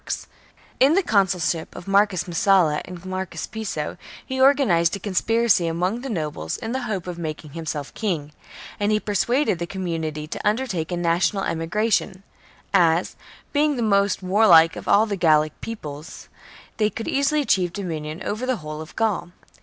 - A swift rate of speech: No, average, 165 wpm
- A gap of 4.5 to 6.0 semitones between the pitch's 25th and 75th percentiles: Yes, average, 4.8 semitones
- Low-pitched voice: No, medium, 185 Hz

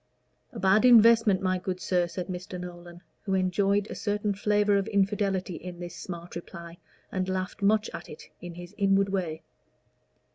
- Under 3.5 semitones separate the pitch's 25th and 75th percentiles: Yes, narrow, 2.4 semitones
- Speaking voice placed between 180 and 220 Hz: Yes, high, 190 Hz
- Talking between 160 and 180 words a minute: Yes, average, 170 wpm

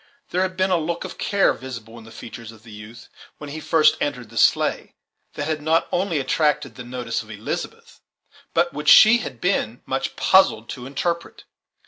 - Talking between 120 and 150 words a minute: No, average, 190 wpm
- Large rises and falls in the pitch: Yes, wide, 6.5 semitones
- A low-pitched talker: No, medium, 145 Hz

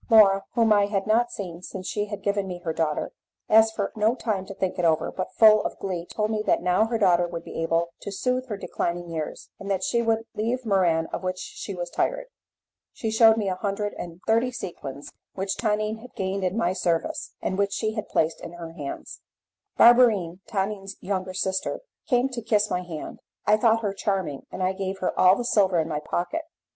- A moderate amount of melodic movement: Yes, average, 3.5 semitones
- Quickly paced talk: Yes, fast, 215 wpm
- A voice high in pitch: Yes, high, 195 Hz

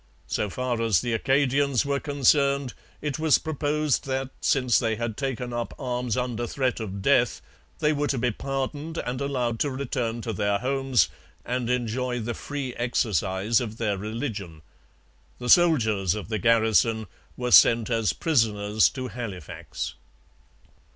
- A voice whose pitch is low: Yes, low, 125 Hz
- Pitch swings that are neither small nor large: Yes, average, 3.5 semitones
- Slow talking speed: No, average, 150 wpm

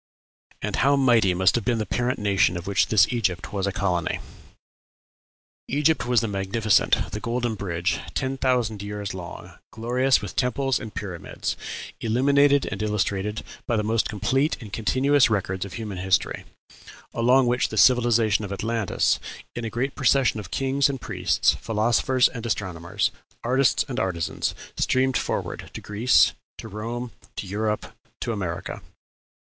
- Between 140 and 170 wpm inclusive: Yes, average, 155 wpm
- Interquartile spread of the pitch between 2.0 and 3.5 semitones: No, average, 4.0 semitones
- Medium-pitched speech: No, low, 110 Hz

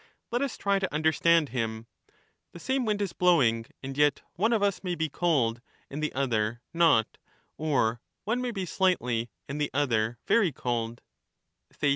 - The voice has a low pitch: No, medium, 150 Hz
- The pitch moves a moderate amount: No, wide, 7.9 semitones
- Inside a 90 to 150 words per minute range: No, average, 165 wpm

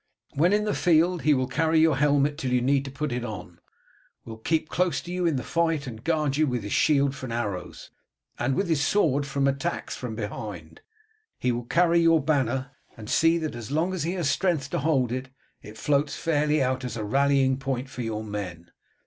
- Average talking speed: No, fast, 215 wpm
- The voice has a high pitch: No, medium, 140 Hz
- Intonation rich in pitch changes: No, average, 4.4 semitones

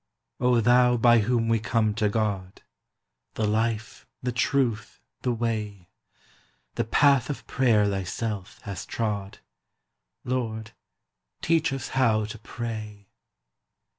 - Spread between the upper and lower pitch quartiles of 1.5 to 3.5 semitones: Yes, average, 2.7 semitones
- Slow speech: Yes, slow, 115 wpm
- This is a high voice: No, low, 115 Hz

